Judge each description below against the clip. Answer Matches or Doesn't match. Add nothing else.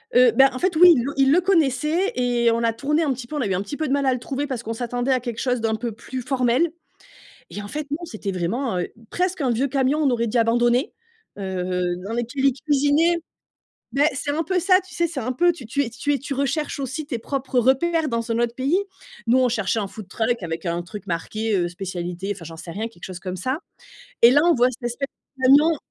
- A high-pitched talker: Matches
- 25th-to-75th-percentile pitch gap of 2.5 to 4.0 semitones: Doesn't match